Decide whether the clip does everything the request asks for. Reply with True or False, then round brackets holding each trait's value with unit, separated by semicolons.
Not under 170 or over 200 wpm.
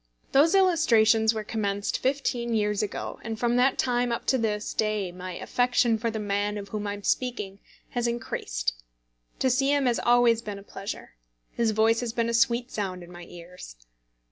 True (190 wpm)